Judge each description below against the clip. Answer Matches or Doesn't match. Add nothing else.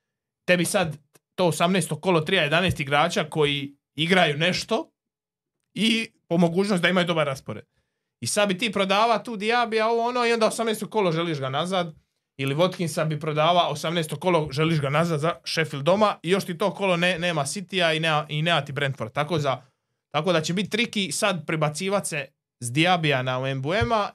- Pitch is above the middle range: Doesn't match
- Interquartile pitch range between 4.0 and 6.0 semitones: Matches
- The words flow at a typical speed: Doesn't match